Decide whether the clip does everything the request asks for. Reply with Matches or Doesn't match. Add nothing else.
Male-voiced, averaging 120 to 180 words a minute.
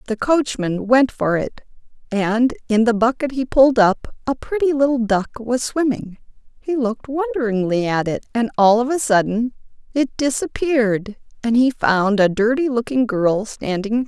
Doesn't match